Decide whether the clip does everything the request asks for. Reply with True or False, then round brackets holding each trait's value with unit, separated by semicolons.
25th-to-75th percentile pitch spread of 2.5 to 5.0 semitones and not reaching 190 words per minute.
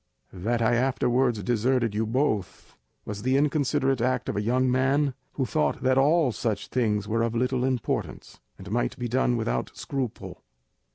True (3.0 semitones; 165 wpm)